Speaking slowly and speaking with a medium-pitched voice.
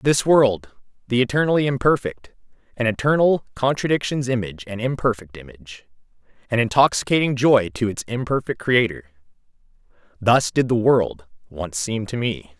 No: slow, 120 wpm; low, 115 Hz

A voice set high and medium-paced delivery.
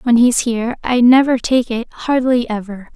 Yes: high, 240 Hz; average, 160 wpm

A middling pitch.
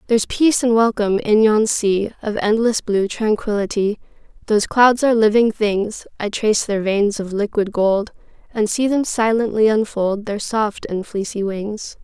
No: high, 215 Hz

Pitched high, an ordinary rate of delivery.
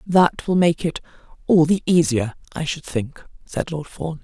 No: medium, 160 Hz; average, 185 wpm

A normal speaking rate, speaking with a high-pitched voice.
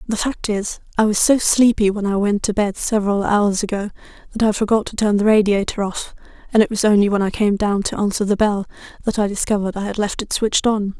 No: fast, 240 wpm; high, 205 Hz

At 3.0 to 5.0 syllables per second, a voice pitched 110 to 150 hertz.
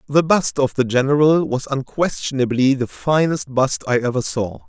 Yes: 4.8 syllables/s; low, 135 Hz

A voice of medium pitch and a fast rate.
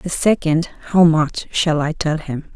No: medium, 160 Hz; average, 190 wpm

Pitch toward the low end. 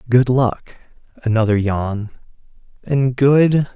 Yes: low, 120 Hz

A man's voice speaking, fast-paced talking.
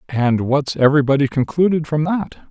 No: male; average, 145 wpm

